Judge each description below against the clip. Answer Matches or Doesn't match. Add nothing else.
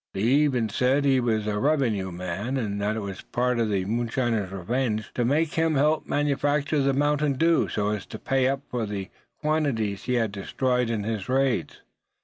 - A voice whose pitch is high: Doesn't match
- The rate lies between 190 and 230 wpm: Matches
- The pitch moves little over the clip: Doesn't match